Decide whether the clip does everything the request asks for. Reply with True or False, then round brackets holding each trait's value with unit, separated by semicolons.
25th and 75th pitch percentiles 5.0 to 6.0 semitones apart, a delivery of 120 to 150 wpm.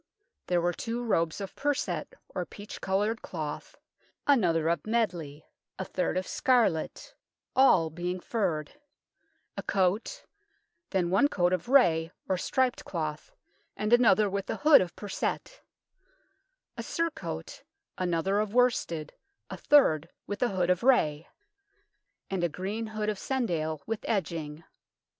True (5.4 semitones; 135 wpm)